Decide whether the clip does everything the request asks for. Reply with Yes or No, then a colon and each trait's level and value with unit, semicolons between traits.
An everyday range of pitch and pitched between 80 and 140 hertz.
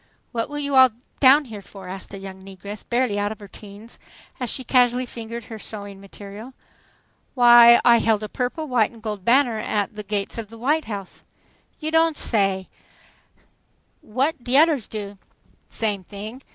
No: average, 3.8 semitones; high, 225 Hz